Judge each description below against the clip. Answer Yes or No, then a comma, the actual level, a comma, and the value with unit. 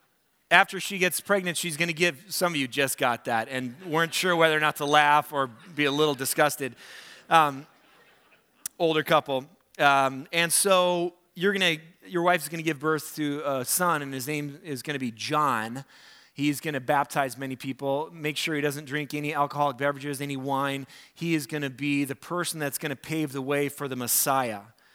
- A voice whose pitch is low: No, medium, 150 Hz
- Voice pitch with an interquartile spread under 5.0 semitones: Yes, average, 3.2 semitones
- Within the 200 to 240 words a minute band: Yes, fast, 205 wpm